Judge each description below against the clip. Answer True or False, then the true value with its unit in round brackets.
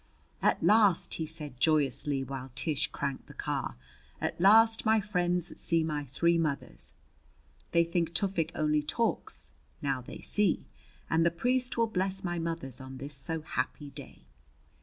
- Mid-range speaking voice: True (165 Hz)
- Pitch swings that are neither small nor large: True (4.7 semitones)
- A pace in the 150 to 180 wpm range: True (155 wpm)